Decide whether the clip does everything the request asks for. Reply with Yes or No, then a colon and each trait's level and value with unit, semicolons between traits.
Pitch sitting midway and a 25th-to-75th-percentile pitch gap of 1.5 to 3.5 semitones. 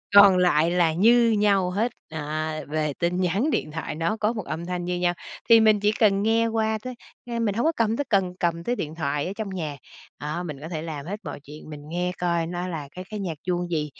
No: medium, 180 Hz; average, 4.7 semitones